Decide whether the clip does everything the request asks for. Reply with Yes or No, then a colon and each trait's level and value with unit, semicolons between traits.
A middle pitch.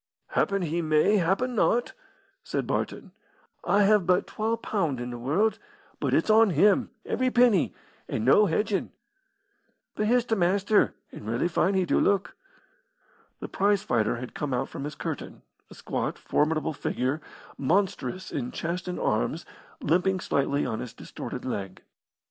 Yes: medium, 180 Hz